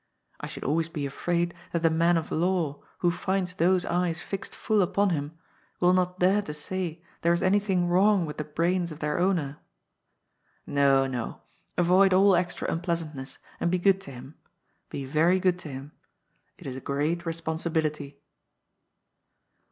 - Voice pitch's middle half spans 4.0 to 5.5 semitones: No, average, 3.3 semitones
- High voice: No, medium, 170 Hz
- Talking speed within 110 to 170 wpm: Yes, average, 165 wpm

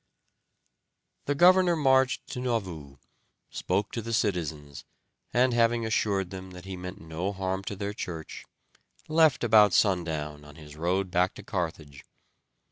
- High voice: No, very low, 95 Hz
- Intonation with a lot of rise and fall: Yes, wide, 5.7 semitones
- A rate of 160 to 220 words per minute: No, average, 140 wpm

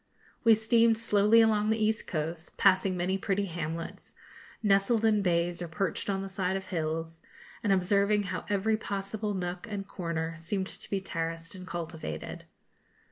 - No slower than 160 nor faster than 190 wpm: Yes, average, 165 wpm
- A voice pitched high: Yes, high, 195 Hz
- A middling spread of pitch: Yes, average, 3.5 semitones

